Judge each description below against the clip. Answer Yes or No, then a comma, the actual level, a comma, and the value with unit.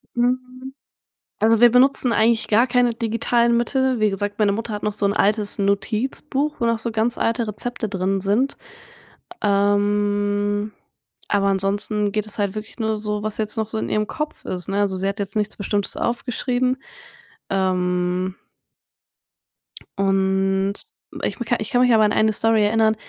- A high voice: Yes, high, 215 Hz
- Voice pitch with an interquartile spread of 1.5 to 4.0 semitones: Yes, average, 2.7 semitones